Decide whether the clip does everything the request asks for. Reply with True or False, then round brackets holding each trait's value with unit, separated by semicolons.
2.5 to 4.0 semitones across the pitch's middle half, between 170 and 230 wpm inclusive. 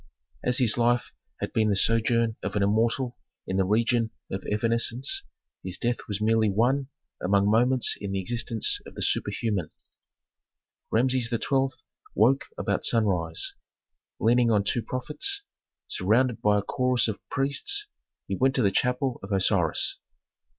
False (3.5 semitones; 145 wpm)